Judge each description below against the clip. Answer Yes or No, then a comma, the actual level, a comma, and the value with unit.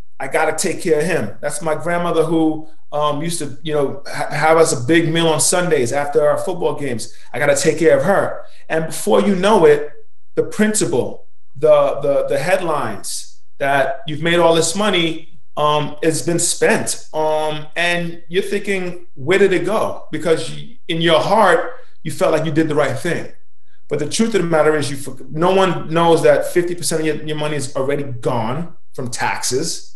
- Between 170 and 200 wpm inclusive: Yes, average, 195 wpm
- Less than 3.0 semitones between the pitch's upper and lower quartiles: Yes, narrow, 2.6 semitones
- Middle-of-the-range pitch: Yes, medium, 160 Hz